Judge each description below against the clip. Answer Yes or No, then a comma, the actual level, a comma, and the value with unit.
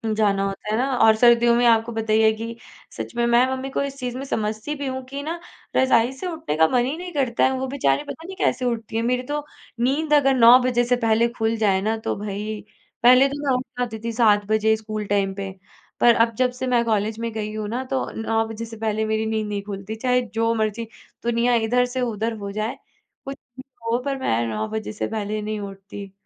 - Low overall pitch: No, high, 230 Hz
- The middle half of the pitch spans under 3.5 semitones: Yes, average, 2.8 semitones